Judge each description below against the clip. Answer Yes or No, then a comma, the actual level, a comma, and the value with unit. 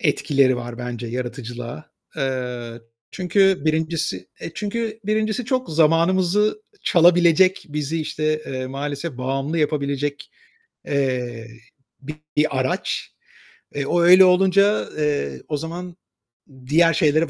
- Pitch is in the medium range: Yes, medium, 155 Hz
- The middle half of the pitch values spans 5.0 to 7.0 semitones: Yes, average, 5.3 semitones